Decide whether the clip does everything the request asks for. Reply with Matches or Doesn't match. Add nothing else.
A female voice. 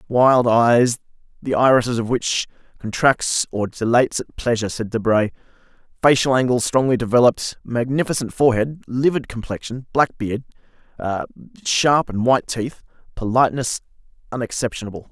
Doesn't match